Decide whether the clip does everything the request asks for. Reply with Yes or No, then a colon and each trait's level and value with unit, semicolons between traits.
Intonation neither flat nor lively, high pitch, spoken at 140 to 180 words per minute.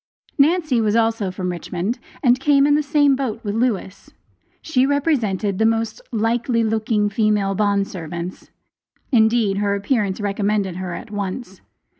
Yes: average, 3.8 semitones; high, 215 Hz; average, 145 wpm